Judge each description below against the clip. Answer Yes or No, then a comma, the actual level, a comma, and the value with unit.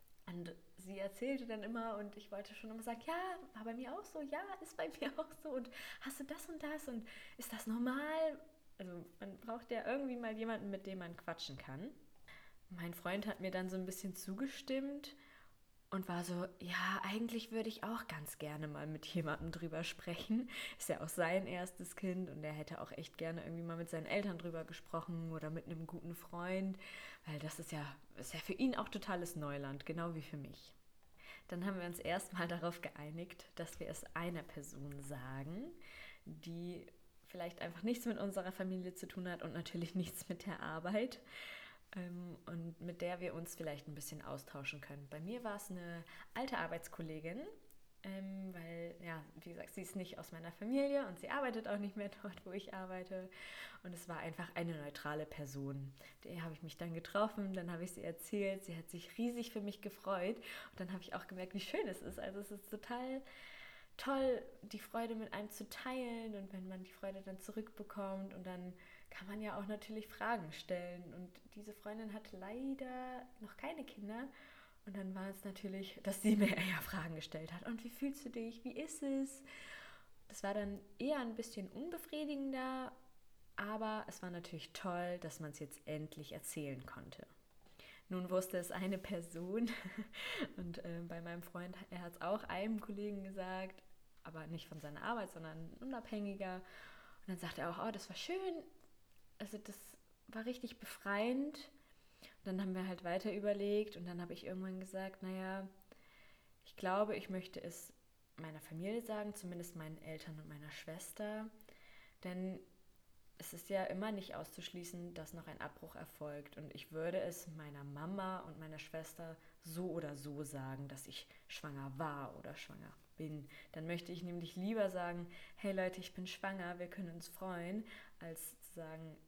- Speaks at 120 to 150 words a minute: No, average, 185 wpm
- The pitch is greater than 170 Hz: Yes, medium, 185 Hz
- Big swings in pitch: No, average, 4.5 semitones